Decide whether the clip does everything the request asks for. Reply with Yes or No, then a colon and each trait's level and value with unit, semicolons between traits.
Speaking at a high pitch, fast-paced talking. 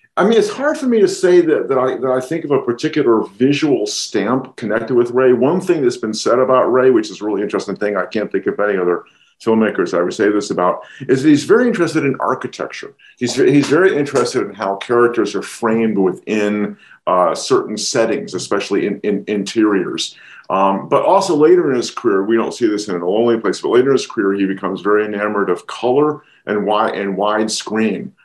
No: low, 130 Hz; fast, 215 wpm